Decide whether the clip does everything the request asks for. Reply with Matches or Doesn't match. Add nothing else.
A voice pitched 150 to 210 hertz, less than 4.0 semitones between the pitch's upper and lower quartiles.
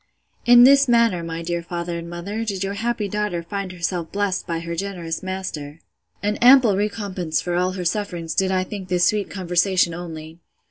Matches